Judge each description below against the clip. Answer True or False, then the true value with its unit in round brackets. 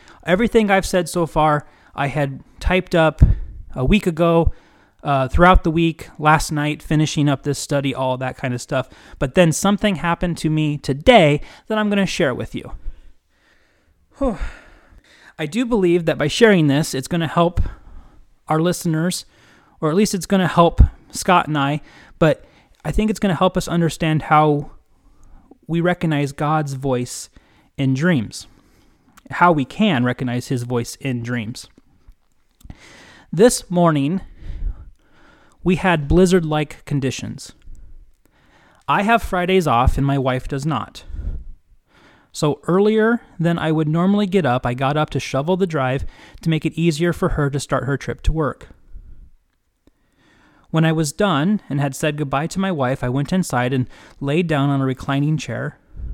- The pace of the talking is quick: False (165 wpm)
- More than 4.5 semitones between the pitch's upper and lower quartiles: True (5.0 semitones)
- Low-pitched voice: False (155 Hz)